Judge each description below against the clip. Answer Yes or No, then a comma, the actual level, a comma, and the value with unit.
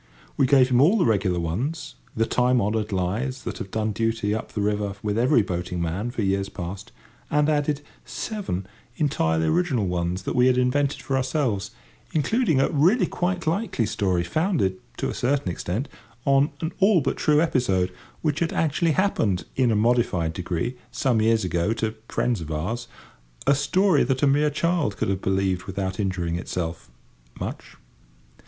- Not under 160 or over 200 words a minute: Yes, average, 165 wpm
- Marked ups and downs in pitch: Yes, wide, 7.2 semitones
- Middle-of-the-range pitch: No, low, 115 Hz